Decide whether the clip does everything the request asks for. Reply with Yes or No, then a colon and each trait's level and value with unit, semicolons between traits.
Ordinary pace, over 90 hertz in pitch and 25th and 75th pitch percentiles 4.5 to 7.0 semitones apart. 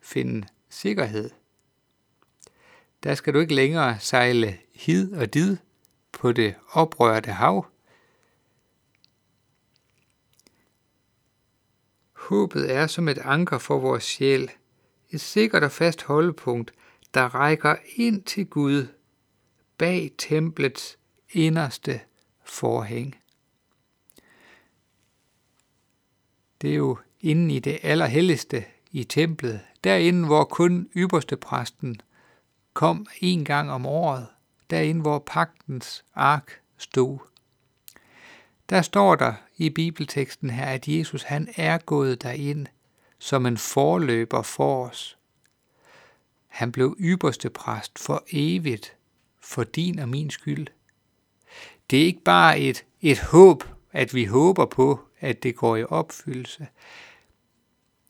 No: slow, 105 wpm; low, 135 Hz; average, 4.9 semitones